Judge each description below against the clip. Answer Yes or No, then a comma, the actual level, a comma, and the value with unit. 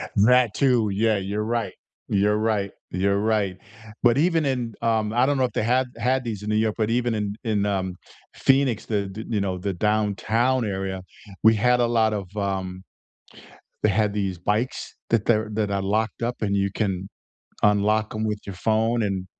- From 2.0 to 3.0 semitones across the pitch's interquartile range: Yes, average, 2.7 semitones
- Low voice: Yes, low, 110 Hz